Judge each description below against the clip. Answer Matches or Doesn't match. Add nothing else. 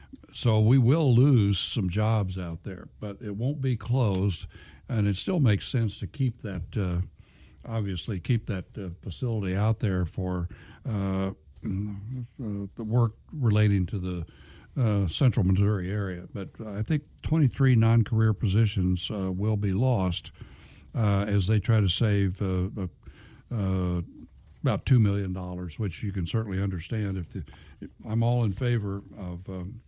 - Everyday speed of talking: Matches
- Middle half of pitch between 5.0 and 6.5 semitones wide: Doesn't match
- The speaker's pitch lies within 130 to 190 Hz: Doesn't match